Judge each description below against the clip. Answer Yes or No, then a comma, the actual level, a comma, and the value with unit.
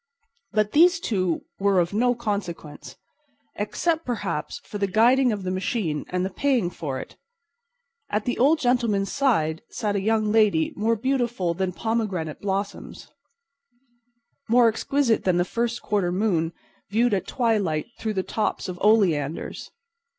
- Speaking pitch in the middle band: No, high, 210 Hz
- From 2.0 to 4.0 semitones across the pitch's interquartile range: No, average, 4.4 semitones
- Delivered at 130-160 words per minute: Yes, average, 145 wpm